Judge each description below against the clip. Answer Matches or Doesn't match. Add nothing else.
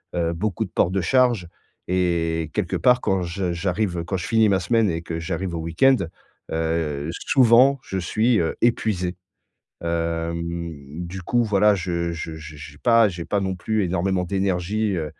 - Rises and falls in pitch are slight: Doesn't match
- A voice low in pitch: Matches